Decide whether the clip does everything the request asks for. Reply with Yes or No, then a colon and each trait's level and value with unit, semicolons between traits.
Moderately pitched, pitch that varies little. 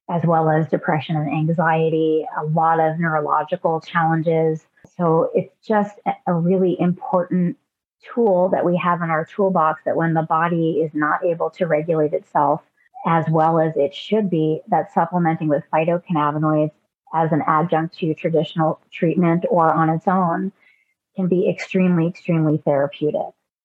Yes: medium, 165 Hz; narrow, 2.1 semitones